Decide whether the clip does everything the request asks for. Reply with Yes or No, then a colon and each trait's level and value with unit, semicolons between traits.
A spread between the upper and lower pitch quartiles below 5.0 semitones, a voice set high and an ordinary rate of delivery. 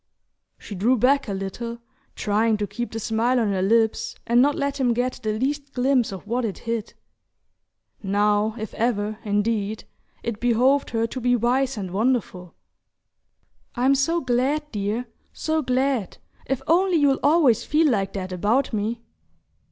Yes: average, 4.0 semitones; high, 235 Hz; average, 160 wpm